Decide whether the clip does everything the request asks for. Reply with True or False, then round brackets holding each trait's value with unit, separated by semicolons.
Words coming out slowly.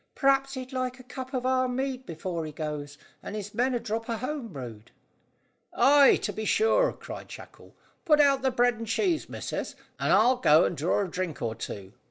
False (205 wpm)